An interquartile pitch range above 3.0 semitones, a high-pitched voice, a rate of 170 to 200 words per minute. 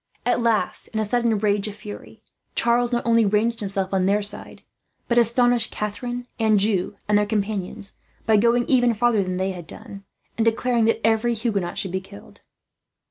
No: average, 2.7 semitones; high, 220 Hz; average, 180 wpm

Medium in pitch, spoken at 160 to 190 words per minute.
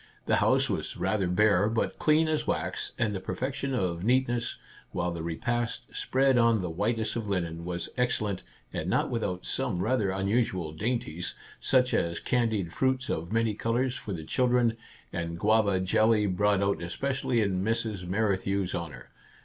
No: low, 105 Hz; average, 170 wpm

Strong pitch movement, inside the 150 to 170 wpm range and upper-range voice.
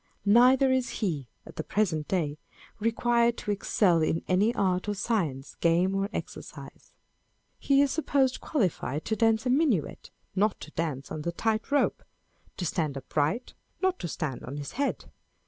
Yes: wide, 7.0 semitones; average, 165 wpm; high, 200 Hz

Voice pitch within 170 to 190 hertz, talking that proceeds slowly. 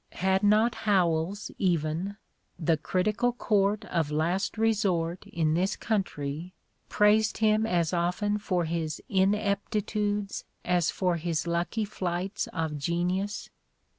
Yes: medium, 185 Hz; slow, 115 wpm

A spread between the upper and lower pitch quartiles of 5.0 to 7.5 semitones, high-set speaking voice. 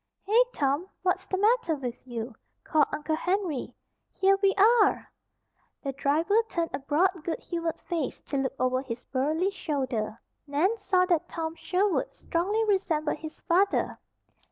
Yes: wide, 5.4 semitones; very high, 330 Hz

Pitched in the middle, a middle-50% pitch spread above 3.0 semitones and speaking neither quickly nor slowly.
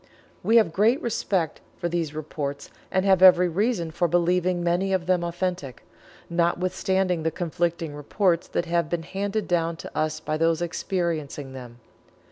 No: medium, 175 Hz; narrow, 2.4 semitones; average, 155 wpm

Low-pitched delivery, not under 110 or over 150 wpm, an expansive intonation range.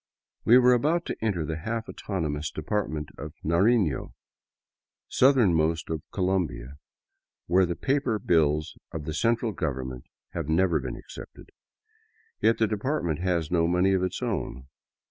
Yes: very low, 85 Hz; average, 140 wpm; wide, 5.9 semitones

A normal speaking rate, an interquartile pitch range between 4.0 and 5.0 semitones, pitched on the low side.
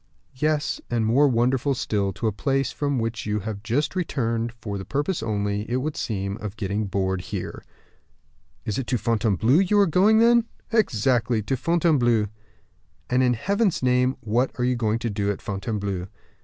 Yes: average, 175 wpm; average, 4.7 semitones; low, 120 Hz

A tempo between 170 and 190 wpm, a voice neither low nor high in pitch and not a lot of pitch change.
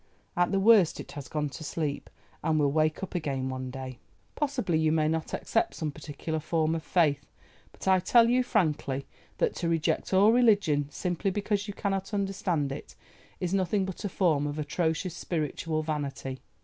No: average, 180 wpm; medium, 160 Hz; average, 4.6 semitones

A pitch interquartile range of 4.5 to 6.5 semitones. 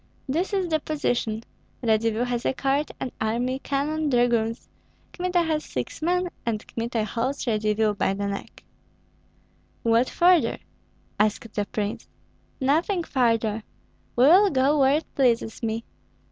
Yes: wide, 5.4 semitones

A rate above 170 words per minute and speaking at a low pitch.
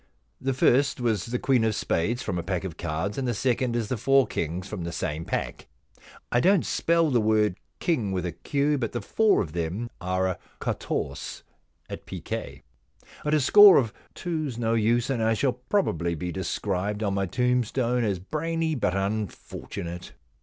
Yes: average, 180 wpm; low, 115 Hz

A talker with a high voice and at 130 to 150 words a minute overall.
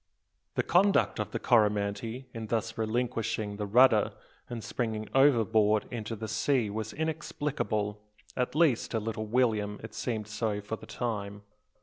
No: low, 110 Hz; average, 145 wpm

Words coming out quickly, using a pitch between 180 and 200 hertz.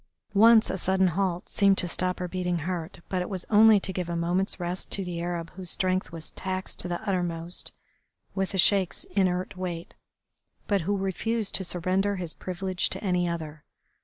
No: average, 190 wpm; medium, 185 Hz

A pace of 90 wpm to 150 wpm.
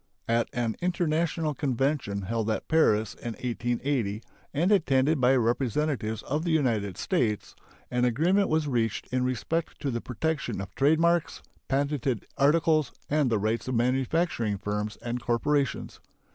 Yes: average, 145 wpm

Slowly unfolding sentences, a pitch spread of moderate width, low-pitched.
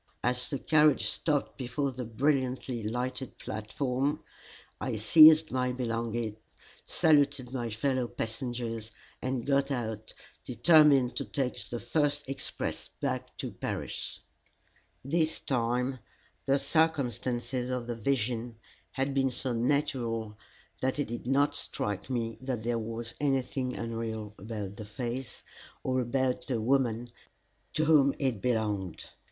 Yes: slow, 125 wpm; average, 3.0 semitones; low, 125 Hz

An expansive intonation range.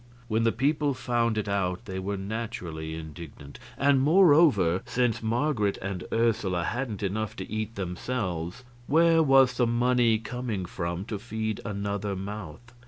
No: average, 4.5 semitones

